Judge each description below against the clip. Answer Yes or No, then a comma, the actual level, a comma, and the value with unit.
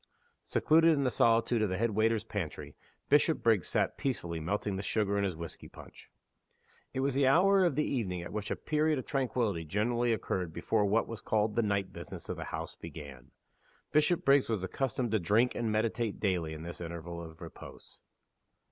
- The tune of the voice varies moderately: No, wide, 5.8 semitones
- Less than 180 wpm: No, average, 185 wpm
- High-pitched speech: No, low, 110 Hz